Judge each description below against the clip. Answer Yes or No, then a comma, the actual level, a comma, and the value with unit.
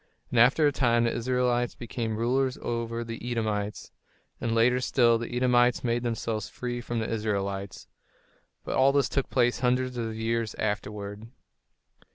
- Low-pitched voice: Yes, low, 115 Hz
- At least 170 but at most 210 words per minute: No, average, 155 wpm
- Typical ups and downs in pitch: No, narrow, 1.8 semitones